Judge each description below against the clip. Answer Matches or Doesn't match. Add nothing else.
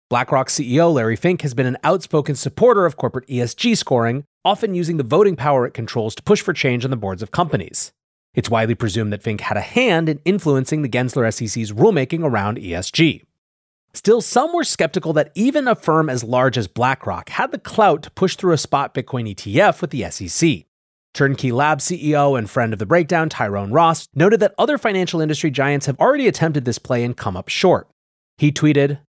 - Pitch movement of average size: Doesn't match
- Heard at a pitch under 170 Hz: Matches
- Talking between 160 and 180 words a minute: Doesn't match